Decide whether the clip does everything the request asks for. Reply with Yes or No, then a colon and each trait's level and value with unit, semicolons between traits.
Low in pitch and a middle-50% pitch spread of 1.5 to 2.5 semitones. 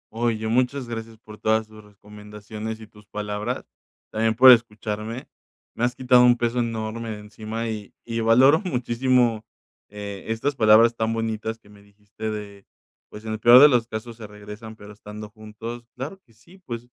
Yes: low, 110 Hz; narrow, 1.9 semitones